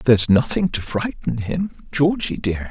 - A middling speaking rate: Yes, average, 155 wpm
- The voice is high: No, medium, 140 Hz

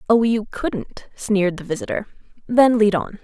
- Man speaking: No, female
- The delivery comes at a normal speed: Yes, average, 165 wpm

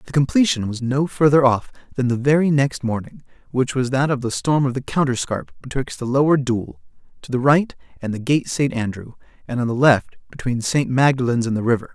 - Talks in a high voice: No, low, 130 Hz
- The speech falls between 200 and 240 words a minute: Yes, fast, 205 wpm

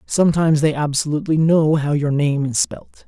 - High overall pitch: No, medium, 150 Hz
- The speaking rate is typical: Yes, average, 175 wpm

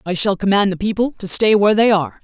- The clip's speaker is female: Yes, female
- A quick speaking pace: Yes, fast, 270 wpm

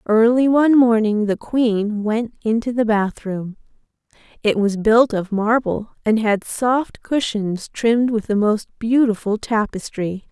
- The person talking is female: Yes, female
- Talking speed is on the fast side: No, average, 140 wpm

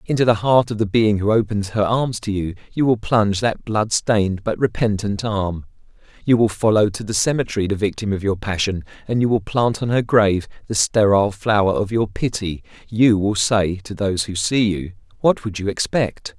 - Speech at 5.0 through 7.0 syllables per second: Yes, 5.2 syllables/s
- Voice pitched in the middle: No, low, 105 Hz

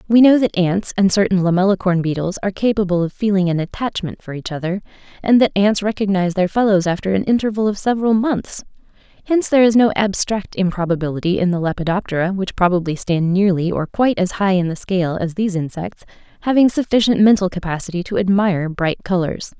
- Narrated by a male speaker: No, female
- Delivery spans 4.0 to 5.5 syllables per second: No, 6.2 syllables/s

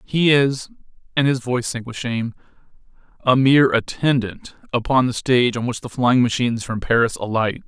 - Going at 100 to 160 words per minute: Yes, average, 155 wpm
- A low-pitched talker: Yes, low, 125 Hz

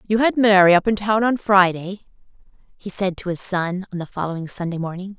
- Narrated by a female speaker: Yes, female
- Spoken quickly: Yes, fast, 210 wpm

